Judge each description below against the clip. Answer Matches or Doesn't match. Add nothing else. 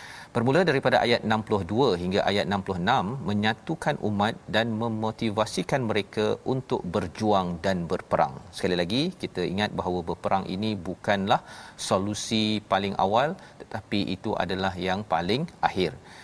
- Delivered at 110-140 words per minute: Matches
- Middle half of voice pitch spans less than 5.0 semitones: Matches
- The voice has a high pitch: Doesn't match